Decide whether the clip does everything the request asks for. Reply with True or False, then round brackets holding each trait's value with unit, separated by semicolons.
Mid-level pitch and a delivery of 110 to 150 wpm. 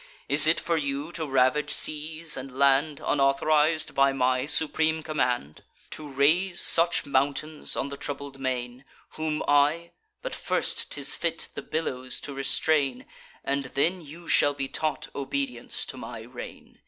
True (145 Hz; 145 wpm)